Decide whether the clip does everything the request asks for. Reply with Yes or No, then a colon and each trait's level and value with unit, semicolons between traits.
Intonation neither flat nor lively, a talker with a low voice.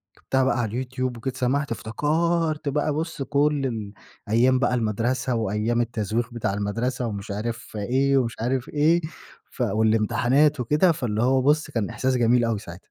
Yes: average, 3.5 semitones; low, 125 Hz